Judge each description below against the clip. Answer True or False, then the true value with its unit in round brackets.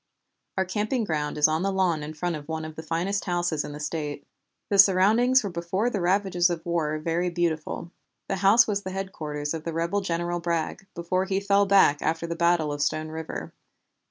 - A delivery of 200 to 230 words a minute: True (205 wpm)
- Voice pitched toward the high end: False (175 Hz)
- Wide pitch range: False (3.4 semitones)